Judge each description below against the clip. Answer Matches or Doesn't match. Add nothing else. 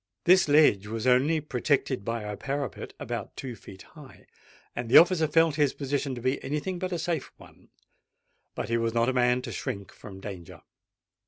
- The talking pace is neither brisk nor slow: Matches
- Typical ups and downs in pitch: Matches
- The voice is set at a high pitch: Doesn't match